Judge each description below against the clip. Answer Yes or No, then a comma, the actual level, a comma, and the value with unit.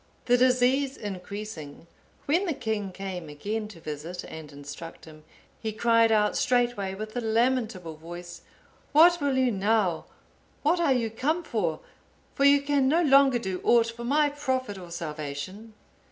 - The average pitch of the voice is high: Yes, high, 220 Hz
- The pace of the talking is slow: No, average, 155 wpm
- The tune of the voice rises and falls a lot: Yes, wide, 6.5 semitones